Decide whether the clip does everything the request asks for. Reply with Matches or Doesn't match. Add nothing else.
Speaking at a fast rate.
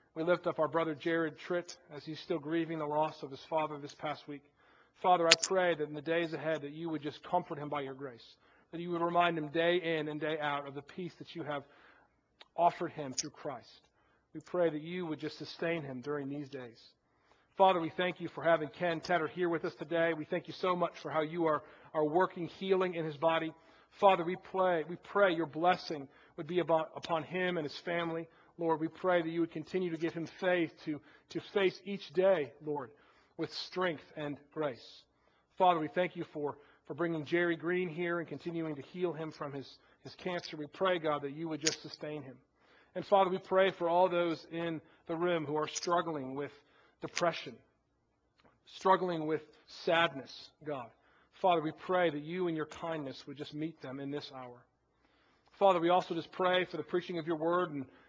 Matches